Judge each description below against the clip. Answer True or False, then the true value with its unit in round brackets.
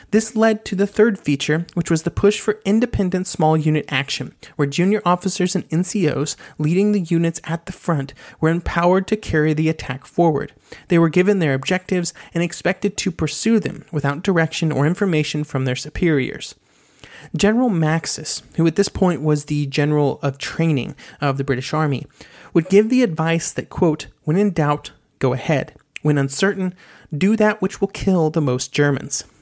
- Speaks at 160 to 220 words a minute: True (175 wpm)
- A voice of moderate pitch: True (165 Hz)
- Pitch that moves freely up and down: False (4.2 semitones)